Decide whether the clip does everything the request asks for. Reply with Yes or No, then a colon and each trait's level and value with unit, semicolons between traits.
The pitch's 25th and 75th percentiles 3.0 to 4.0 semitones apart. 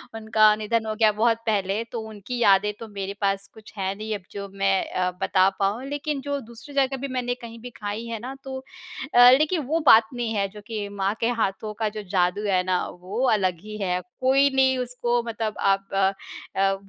Yes: average, 3.5 semitones